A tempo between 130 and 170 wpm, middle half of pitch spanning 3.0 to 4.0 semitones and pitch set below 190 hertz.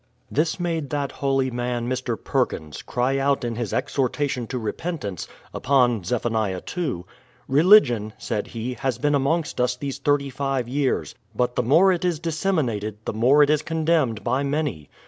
Yes: average, 165 wpm; average, 3.5 semitones; low, 135 Hz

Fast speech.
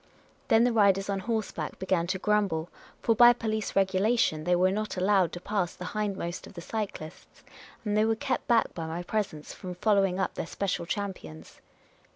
No: average, 185 wpm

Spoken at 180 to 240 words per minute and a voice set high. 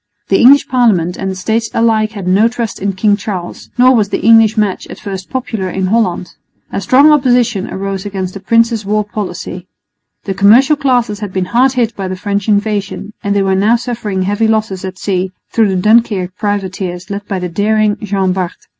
Yes: average, 200 wpm; high, 205 Hz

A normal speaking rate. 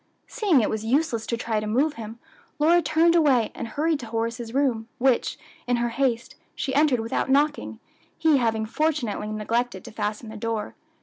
Yes: average, 180 wpm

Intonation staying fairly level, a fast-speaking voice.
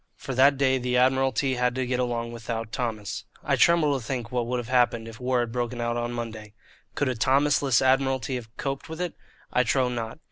Yes: narrow, 2.0 semitones; fast, 215 wpm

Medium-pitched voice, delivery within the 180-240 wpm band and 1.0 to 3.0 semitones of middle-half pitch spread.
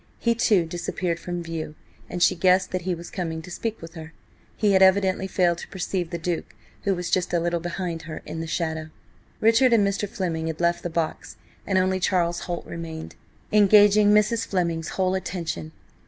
Yes: medium, 175 Hz; average, 195 wpm; narrow, 2.4 semitones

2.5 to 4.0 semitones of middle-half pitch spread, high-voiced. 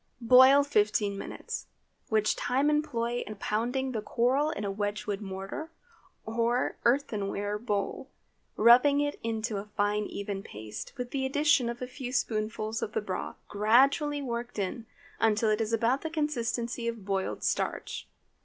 Yes: average, 3.7 semitones; high, 230 Hz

